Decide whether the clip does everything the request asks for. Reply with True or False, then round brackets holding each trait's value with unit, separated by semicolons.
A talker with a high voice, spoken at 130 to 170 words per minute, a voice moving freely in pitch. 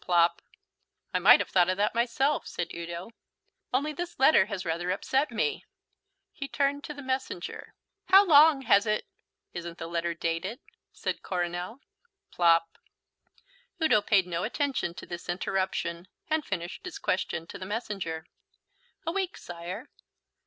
True (195 Hz; 150 wpm; 8.1 semitones)